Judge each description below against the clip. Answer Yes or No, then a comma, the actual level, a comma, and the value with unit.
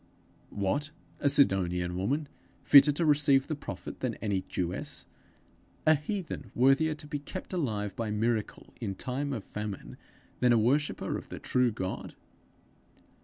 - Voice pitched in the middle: No, low, 125 Hz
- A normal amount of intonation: No, wide, 5.9 semitones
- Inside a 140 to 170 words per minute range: Yes, average, 145 wpm